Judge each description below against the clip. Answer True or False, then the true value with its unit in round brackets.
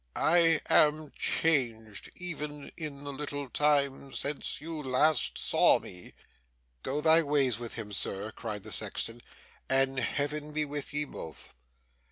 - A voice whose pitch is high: False (145 Hz)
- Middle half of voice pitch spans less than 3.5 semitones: True (2.9 semitones)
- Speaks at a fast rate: False (140 wpm)